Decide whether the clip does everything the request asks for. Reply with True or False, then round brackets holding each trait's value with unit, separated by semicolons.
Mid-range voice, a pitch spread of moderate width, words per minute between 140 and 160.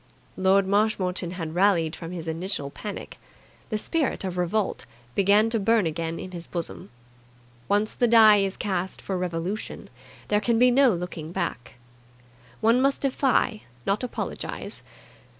False (195 Hz; 3.9 semitones; 145 wpm)